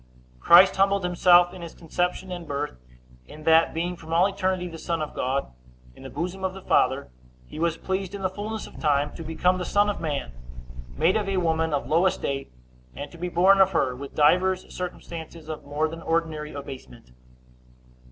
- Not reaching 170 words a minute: No, average, 195 wpm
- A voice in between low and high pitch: Yes, medium, 170 Hz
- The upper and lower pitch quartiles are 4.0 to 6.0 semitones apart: No, average, 3.5 semitones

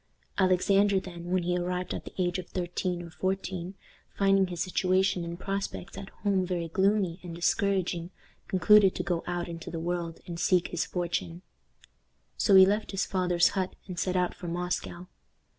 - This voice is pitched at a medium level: Yes, medium, 180 Hz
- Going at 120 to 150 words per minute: No, average, 175 wpm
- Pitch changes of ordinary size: No, narrow, 1.7 semitones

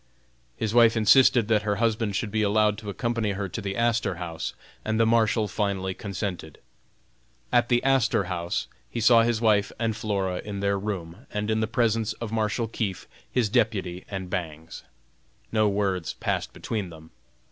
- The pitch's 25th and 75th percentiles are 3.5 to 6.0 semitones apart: No, average, 2.7 semitones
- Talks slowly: No, average, 170 wpm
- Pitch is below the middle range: Yes, low, 105 Hz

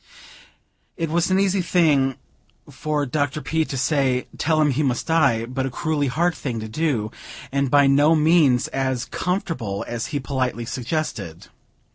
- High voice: No, medium, 140 Hz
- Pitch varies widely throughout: No, average, 4.0 semitones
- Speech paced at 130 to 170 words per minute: Yes, average, 160 wpm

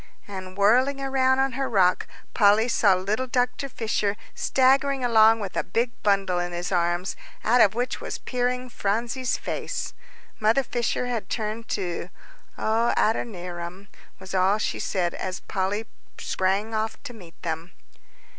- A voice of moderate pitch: No, high, 215 Hz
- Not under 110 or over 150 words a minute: Yes, average, 145 wpm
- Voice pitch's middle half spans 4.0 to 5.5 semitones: Yes, average, 4.7 semitones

